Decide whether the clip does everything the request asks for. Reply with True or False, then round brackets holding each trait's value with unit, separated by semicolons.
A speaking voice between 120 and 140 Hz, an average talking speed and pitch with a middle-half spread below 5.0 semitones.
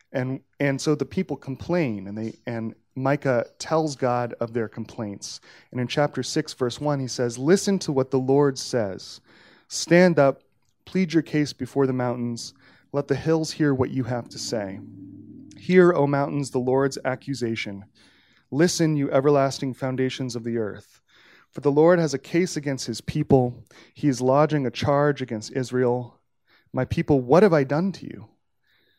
True (135 Hz; 170 wpm; 3.3 semitones)